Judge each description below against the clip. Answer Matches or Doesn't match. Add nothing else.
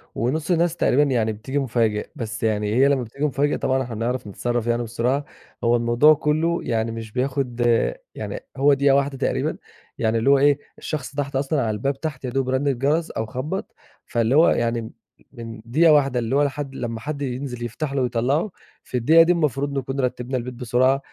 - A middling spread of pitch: Matches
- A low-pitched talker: Matches